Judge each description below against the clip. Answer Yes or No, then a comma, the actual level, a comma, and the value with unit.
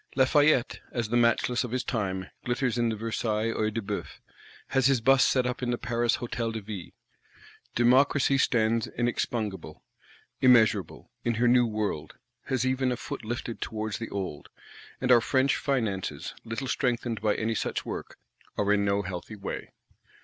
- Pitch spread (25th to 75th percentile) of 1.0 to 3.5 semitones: Yes, average, 2.7 semitones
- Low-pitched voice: Yes, low, 115 Hz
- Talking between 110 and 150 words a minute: No, average, 160 wpm